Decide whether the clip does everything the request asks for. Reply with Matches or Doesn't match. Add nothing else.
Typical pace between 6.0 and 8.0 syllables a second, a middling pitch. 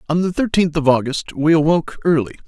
Matches